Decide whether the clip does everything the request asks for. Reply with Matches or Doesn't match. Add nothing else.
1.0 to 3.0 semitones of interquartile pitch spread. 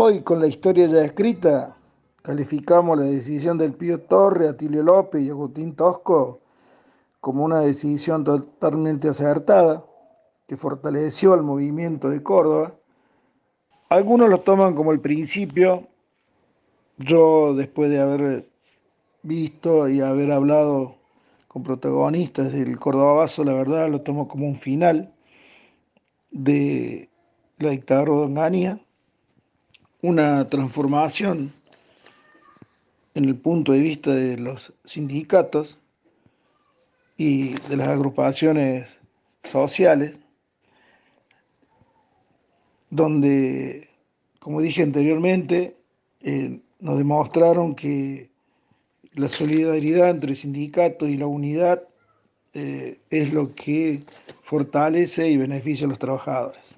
Matches